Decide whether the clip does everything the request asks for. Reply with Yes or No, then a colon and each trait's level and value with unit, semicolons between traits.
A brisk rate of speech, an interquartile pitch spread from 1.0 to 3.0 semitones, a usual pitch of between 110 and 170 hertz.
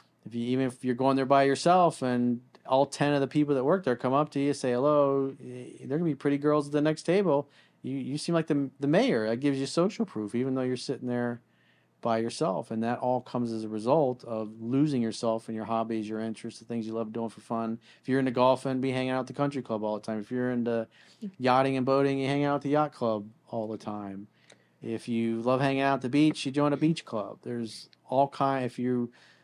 No: fast, 250 wpm; average, 3.4 semitones; low, 130 Hz